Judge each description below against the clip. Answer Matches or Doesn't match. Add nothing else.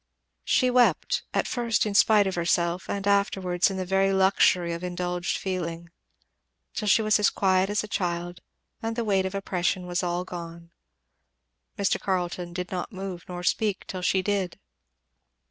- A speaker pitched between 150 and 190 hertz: Matches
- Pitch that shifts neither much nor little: Doesn't match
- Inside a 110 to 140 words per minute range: Doesn't match